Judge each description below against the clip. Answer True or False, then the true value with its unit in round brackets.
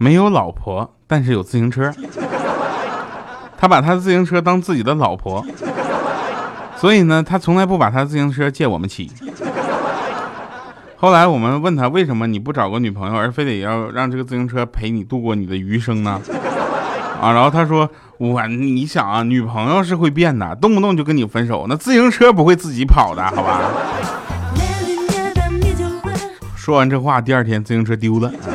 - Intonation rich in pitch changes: True (6.9 semitones)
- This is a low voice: True (130 Hz)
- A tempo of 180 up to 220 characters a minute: False (255 characters per minute)